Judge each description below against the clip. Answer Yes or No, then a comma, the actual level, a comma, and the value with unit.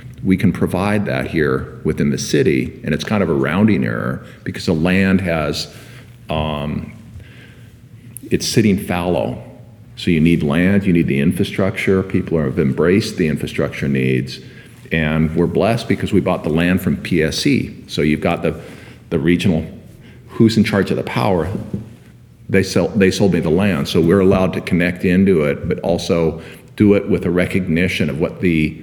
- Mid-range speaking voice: No, very low, 95 Hz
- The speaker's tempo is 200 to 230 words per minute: No, average, 175 wpm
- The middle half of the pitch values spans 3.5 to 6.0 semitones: Yes, average, 4.0 semitones